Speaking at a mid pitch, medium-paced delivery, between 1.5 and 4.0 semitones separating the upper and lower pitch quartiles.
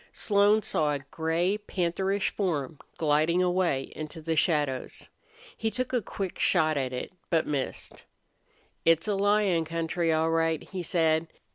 Yes: medium, 165 Hz; average, 145 wpm; average, 3.4 semitones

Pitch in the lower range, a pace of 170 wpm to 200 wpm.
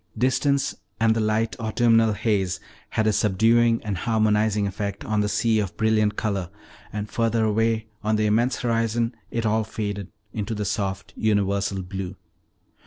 No: low, 110 Hz; average, 155 wpm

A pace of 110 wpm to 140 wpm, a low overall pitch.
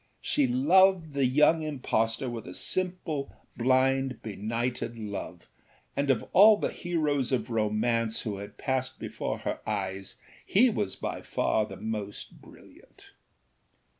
Yes: slow, 135 wpm; low, 130 Hz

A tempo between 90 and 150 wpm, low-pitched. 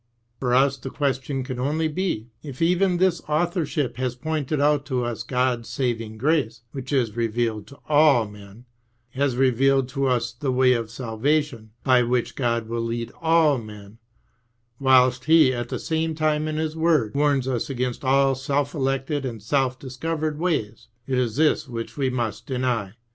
No: average, 170 wpm; low, 130 Hz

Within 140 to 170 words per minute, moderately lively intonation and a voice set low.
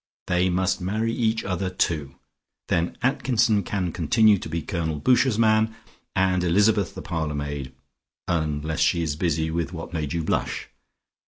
Yes: average, 155 wpm; average, 4.7 semitones; very low, 90 Hz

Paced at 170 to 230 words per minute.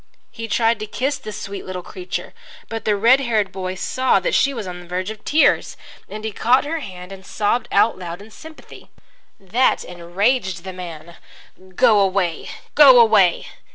Yes: average, 180 wpm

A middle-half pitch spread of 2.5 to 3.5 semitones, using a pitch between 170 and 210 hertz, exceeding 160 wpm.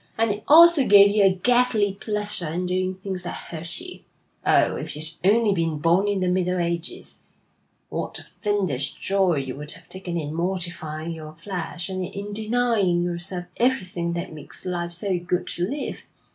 Yes: average, 3.1 semitones; medium, 185 Hz; average, 175 wpm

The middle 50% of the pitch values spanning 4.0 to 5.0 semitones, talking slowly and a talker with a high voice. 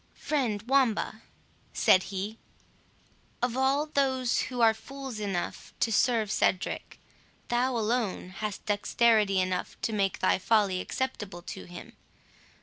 Yes: average, 4.3 semitones; slow, 125 wpm; high, 220 Hz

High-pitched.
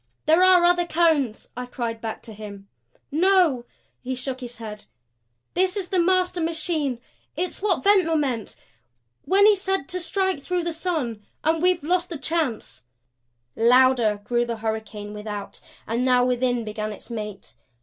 Yes: very high, 260 Hz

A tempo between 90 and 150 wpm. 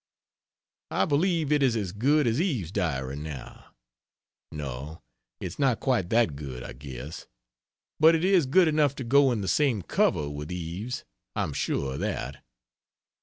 No: average, 160 wpm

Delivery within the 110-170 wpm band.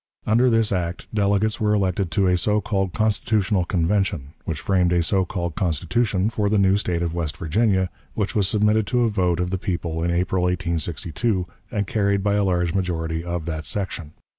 No: average, 190 wpm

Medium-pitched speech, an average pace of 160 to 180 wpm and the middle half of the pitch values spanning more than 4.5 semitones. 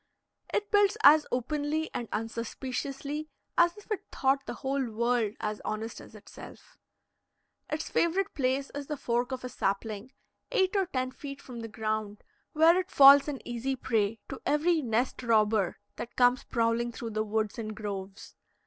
No: very high, 255 Hz; average, 165 wpm; average, 4.9 semitones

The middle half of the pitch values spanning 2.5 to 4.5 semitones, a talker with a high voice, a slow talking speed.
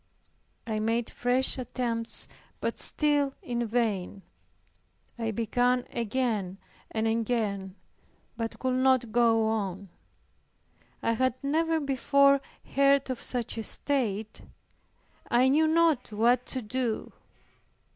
Yes: average, 3.0 semitones; high, 240 Hz; slow, 110 wpm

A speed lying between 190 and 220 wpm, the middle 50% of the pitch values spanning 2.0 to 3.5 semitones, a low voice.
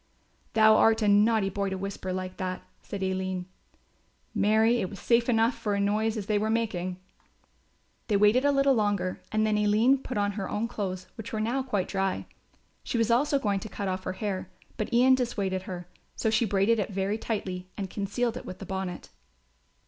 No: average, 200 wpm; average, 2.9 semitones; high, 205 Hz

